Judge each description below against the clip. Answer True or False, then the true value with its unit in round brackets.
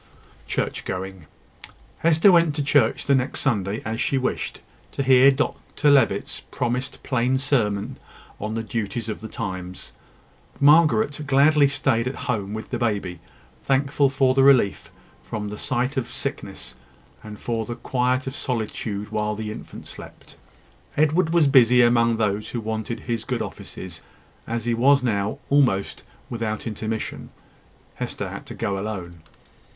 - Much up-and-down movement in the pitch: False (4.2 semitones)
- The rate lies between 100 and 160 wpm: True (150 wpm)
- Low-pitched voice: True (120 Hz)